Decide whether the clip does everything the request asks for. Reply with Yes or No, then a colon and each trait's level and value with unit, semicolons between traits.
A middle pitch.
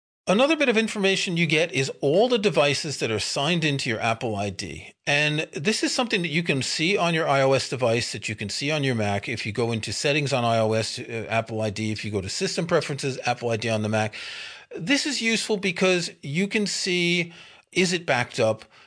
Yes: medium, 145 Hz